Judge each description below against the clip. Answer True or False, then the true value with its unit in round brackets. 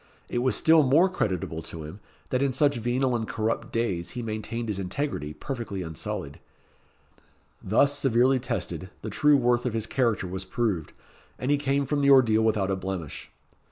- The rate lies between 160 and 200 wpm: True (175 wpm)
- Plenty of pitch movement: True (5.8 semitones)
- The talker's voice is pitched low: True (115 Hz)